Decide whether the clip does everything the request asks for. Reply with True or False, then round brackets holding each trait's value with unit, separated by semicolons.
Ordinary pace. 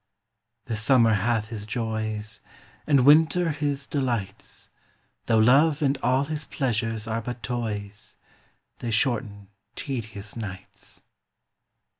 False (110 wpm)